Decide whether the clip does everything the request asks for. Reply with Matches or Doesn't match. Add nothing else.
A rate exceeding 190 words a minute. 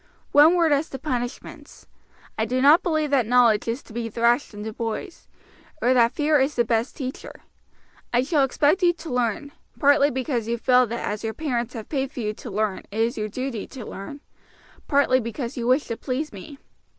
Matches